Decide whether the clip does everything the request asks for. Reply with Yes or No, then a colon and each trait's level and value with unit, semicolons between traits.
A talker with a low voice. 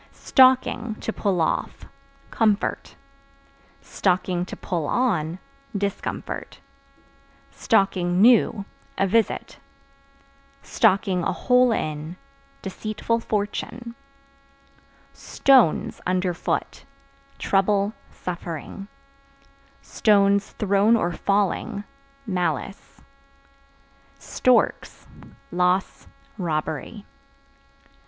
No: high, 195 Hz